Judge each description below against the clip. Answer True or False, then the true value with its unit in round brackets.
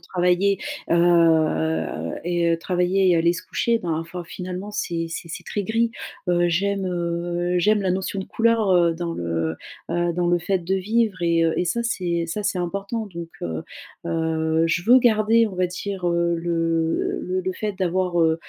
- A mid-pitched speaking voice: True (175 Hz)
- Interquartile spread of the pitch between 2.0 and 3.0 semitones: True (2.5 semitones)